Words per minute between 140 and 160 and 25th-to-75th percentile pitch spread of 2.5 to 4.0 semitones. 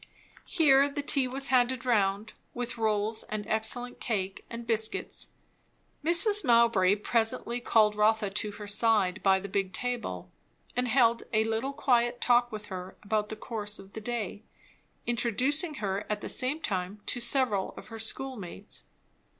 Yes: average, 155 wpm; average, 3.0 semitones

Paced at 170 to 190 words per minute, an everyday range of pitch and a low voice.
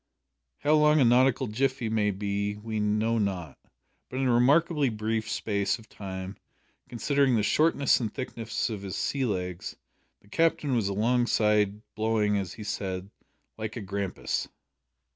No: average, 150 wpm; average, 3.8 semitones; low, 110 Hz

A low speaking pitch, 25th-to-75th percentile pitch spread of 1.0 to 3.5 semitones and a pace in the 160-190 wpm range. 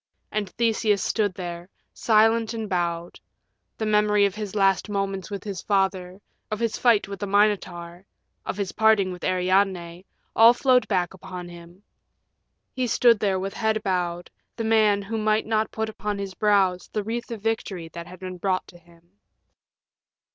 No: high, 200 Hz; average, 3.0 semitones; average, 170 wpm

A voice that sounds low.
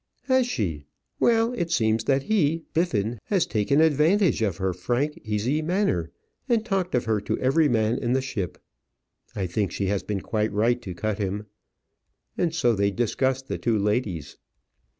Yes: low, 120 Hz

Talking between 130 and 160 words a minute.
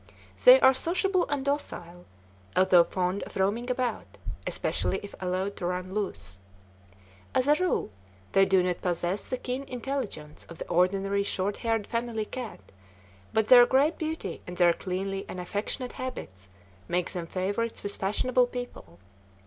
Yes: average, 150 wpm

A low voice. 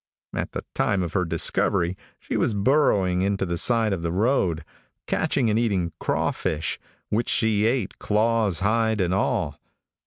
Yes: low, 100 Hz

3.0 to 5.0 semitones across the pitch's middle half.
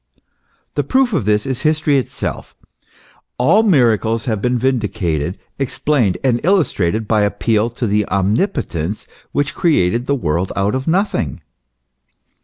No: wide, 5.6 semitones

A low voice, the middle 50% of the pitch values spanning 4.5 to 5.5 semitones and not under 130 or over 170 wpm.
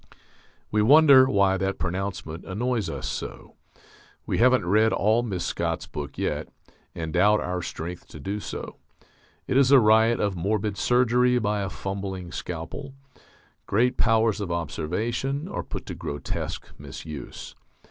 Yes: low, 105 Hz; average, 5.1 semitones; average, 145 wpm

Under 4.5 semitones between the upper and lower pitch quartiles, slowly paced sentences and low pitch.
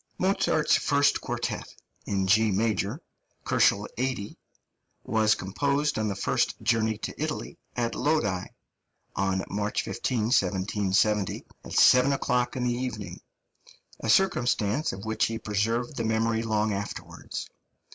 Yes: average, 3.5 semitones; slow, 125 wpm; low, 110 Hz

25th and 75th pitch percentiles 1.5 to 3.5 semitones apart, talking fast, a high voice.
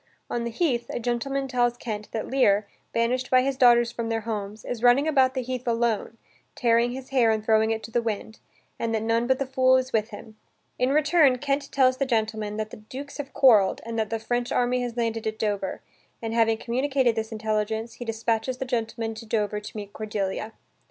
Yes: narrow, 2.6 semitones; fast, 210 wpm; high, 230 Hz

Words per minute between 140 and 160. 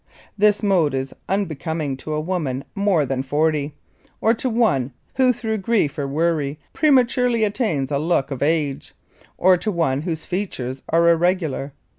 Yes: average, 155 wpm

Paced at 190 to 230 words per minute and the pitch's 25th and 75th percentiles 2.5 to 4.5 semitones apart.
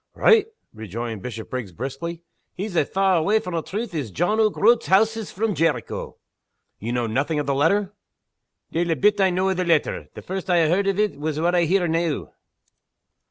No: fast, 205 wpm; wide, 5.6 semitones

